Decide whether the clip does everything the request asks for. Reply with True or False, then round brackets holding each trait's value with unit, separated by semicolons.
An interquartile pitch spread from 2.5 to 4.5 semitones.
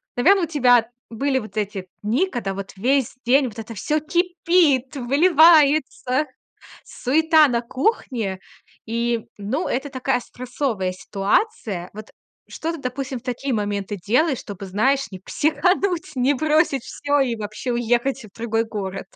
False (5.2 semitones)